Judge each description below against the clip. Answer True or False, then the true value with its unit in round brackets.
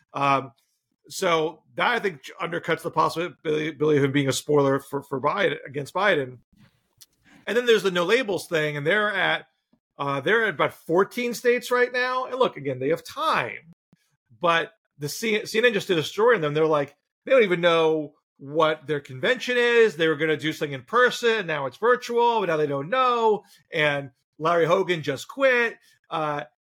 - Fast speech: False (190 wpm)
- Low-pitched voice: False (160 Hz)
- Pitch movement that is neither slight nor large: False (7.5 semitones)